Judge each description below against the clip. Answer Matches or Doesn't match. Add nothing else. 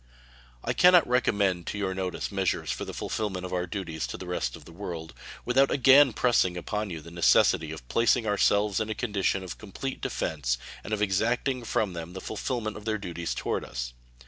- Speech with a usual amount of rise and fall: Matches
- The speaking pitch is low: Matches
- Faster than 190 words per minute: Matches